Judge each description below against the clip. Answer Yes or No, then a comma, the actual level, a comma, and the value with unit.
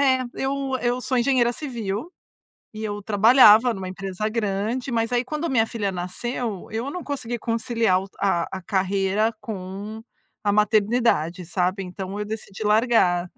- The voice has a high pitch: Yes, high, 215 Hz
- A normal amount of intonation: Yes, average, 3.8 semitones